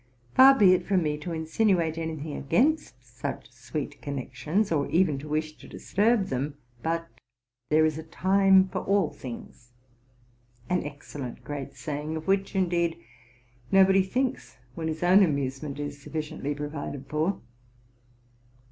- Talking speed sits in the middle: Yes, average, 150 wpm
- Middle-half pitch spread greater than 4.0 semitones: Yes, average, 4.7 semitones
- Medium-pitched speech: Yes, medium, 160 Hz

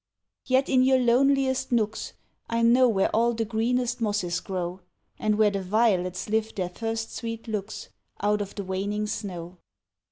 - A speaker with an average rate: Yes, average, 160 wpm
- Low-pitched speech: No, high, 220 Hz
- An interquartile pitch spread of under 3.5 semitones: Yes, average, 3.0 semitones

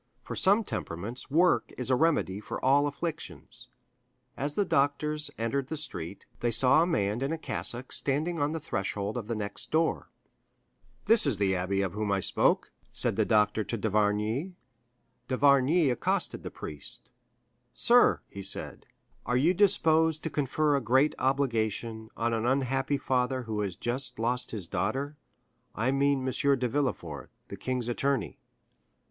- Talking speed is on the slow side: No, average, 160 wpm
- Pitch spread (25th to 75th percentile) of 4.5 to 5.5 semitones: Yes, average, 5.2 semitones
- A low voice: Yes, low, 130 Hz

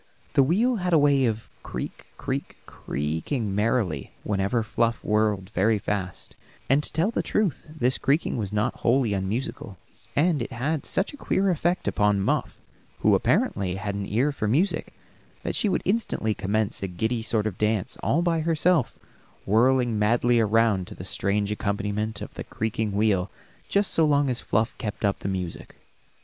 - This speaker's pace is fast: No, average, 170 wpm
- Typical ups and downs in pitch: No, wide, 5.8 semitones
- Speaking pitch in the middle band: No, low, 110 Hz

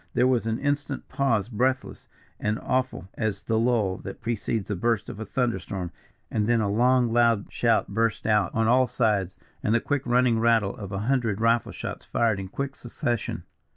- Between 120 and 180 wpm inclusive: No, average, 190 wpm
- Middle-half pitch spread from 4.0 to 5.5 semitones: No, average, 2.7 semitones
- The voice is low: Yes, low, 115 Hz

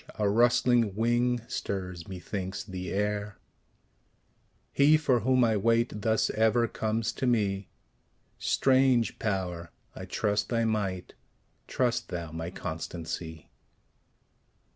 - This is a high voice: No, low, 105 Hz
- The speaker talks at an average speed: No, slow, 110 wpm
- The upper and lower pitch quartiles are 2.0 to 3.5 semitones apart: No, average, 4.1 semitones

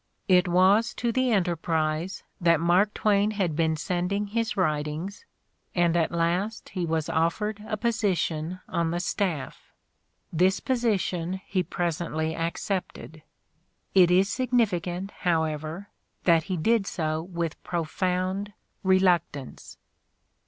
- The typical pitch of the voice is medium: Yes, medium, 180 Hz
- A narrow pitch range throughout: No, average, 3.3 semitones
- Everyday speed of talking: No, slow, 120 wpm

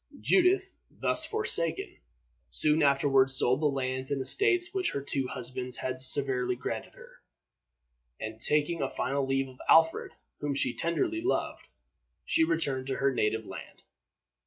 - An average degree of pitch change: Yes, average, 4.1 semitones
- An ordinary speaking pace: Yes, average, 145 wpm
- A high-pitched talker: No, medium, 140 Hz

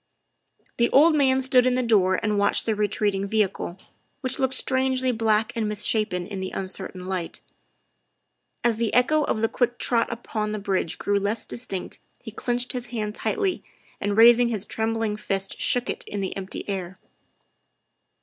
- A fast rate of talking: No, average, 175 wpm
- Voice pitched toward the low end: No, high, 220 Hz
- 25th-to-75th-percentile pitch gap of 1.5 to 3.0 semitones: No, average, 3.5 semitones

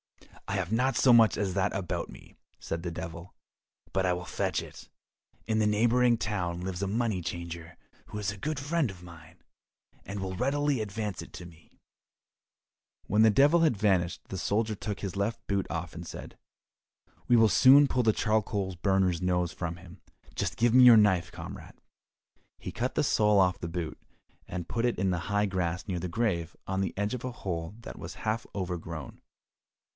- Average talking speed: Yes, average, 195 wpm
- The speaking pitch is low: Yes, low, 100 Hz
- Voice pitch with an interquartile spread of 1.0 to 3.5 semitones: No, average, 4.1 semitones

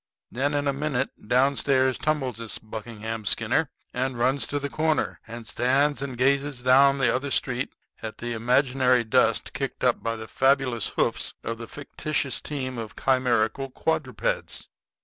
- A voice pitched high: No, low, 130 Hz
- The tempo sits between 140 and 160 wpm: Yes, average, 155 wpm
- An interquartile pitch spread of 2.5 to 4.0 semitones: Yes, average, 2.9 semitones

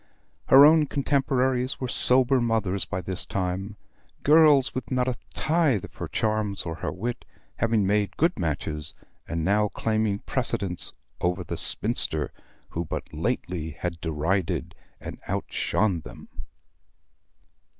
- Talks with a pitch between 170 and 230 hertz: No, low, 105 Hz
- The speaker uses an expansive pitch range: Yes, wide, 6.2 semitones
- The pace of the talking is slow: Yes, slow, 130 wpm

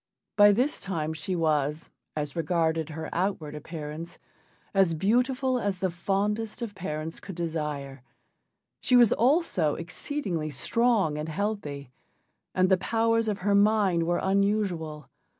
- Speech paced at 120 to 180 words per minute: Yes, slow, 135 wpm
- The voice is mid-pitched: Yes, medium, 180 Hz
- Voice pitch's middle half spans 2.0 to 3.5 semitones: No, average, 5.0 semitones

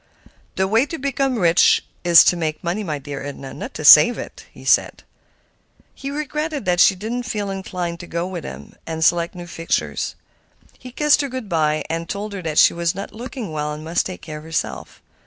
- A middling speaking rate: No, fast, 210 wpm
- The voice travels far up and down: Yes, wide, 5.8 semitones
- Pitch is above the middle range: No, medium, 175 Hz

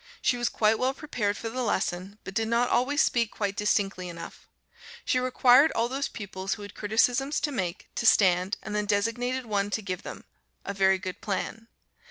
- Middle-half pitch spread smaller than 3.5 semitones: No, average, 3.9 semitones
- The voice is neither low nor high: No, high, 215 Hz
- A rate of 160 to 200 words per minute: Yes, average, 195 wpm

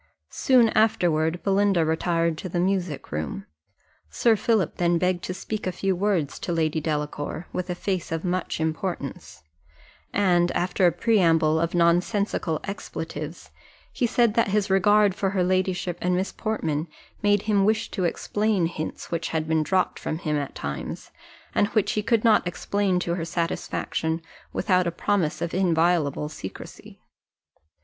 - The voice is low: No, medium, 180 Hz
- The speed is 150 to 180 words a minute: Yes, average, 155 wpm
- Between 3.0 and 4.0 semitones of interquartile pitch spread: Yes, average, 3.6 semitones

